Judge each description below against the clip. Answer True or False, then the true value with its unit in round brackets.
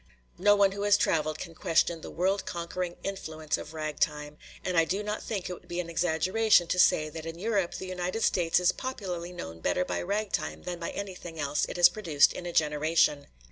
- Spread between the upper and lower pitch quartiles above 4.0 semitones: False (3.3 semitones)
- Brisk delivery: True (210 wpm)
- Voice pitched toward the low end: False (175 Hz)